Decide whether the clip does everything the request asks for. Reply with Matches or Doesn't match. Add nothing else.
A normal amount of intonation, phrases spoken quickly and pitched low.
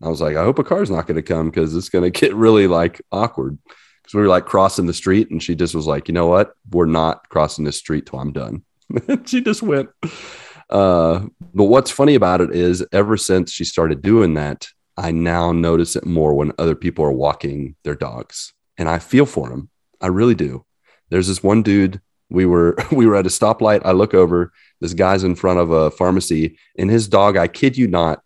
Matches